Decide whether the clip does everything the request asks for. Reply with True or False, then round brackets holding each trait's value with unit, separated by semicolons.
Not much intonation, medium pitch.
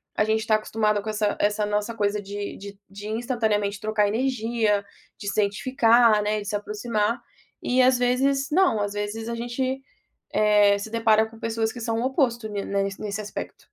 False (2.2 semitones; 215 Hz)